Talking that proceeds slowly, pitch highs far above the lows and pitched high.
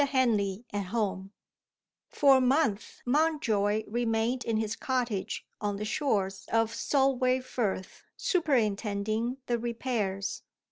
No: slow, 120 wpm; average, 3.9 semitones; high, 225 Hz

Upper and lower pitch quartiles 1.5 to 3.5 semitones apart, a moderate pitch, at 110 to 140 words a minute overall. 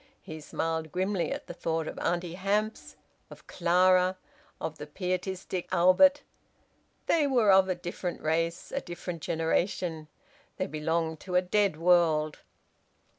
Yes: narrow, 2.5 semitones; medium, 175 Hz; slow, 135 wpm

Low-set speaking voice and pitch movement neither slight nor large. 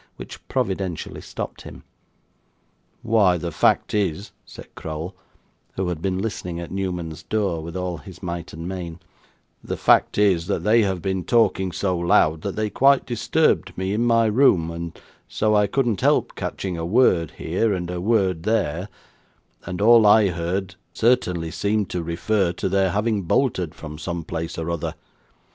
Yes: very low, 95 Hz; average, 3.7 semitones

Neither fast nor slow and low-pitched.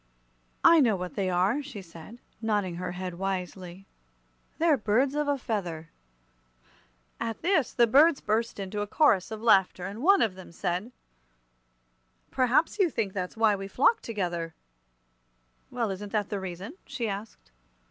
No: average, 155 wpm; high, 205 Hz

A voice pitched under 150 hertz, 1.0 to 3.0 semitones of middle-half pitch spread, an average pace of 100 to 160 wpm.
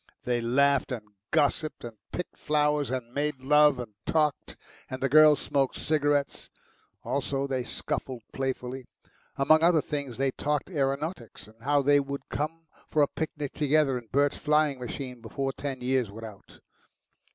Yes: medium, 140 Hz; average, 2.7 semitones; average, 155 wpm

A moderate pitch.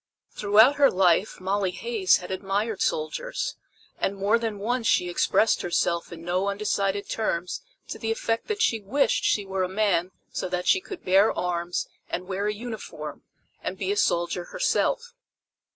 No: high, 200 Hz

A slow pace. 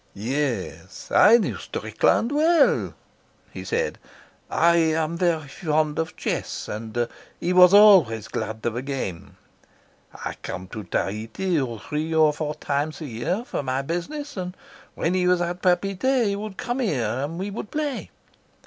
No: average, 155 wpm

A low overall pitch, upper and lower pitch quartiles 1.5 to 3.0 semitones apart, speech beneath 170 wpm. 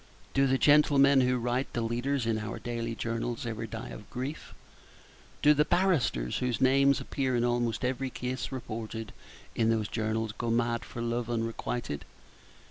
Yes: low, 120 Hz; narrow, 2.5 semitones; average, 160 wpm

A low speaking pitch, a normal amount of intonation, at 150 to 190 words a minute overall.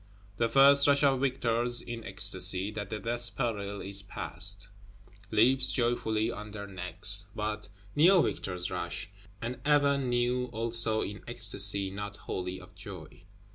No: low, 110 Hz; average, 3.5 semitones; average, 140 wpm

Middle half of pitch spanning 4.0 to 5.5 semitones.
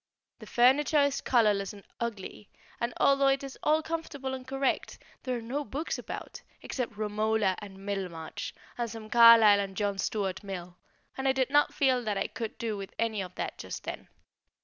Yes: average, 4.8 semitones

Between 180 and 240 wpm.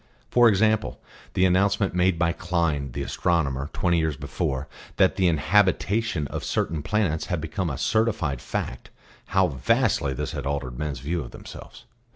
No: average, 160 wpm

